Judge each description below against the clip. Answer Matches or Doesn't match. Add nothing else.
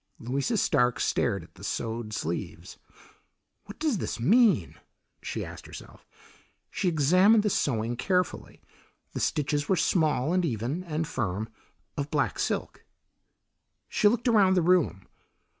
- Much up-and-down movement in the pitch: Matches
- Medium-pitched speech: Matches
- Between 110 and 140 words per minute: Matches